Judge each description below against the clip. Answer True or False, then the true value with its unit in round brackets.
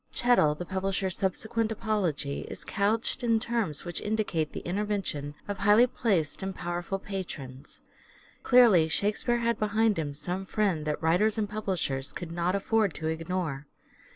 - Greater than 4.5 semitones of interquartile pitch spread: True (5.0 semitones)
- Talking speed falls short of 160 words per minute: True (150 wpm)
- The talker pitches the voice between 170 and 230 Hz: True (190 Hz)